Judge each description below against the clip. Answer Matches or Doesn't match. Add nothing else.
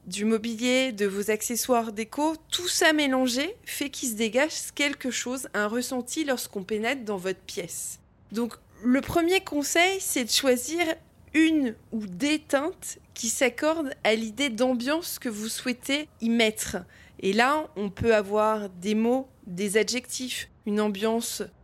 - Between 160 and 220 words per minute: Doesn't match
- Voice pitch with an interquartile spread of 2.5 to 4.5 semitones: Doesn't match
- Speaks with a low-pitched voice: Doesn't match